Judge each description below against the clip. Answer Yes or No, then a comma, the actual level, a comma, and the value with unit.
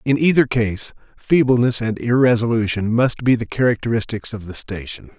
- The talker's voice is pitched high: No, low, 115 Hz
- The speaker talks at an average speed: Yes, average, 150 wpm